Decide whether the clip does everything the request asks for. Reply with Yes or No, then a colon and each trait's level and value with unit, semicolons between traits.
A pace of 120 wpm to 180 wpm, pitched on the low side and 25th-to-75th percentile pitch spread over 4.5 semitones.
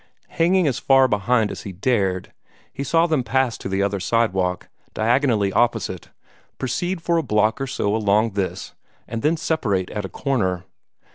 Yes: average, 165 wpm; low, 115 Hz; average, 5.3 semitones